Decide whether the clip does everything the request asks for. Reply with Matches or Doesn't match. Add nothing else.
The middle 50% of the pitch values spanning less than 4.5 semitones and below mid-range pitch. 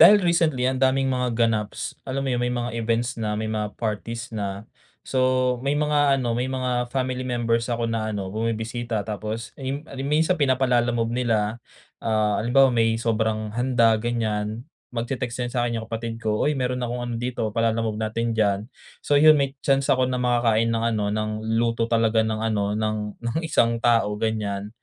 Matches